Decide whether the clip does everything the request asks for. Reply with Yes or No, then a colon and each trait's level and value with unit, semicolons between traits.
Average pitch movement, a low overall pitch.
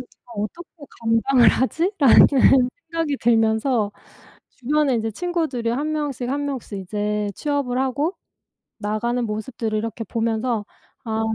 No: average, 4.3 semitones; high, 245 Hz